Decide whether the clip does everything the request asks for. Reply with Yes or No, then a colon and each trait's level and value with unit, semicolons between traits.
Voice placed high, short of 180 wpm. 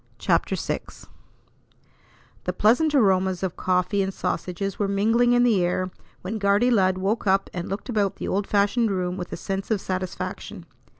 Yes: high, 195 Hz; average, 170 wpm